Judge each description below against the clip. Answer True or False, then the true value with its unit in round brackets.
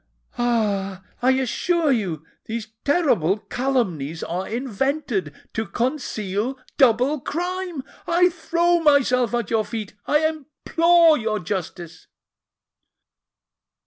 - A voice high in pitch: True (245 Hz)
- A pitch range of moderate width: False (6.8 semitones)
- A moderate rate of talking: False (95 wpm)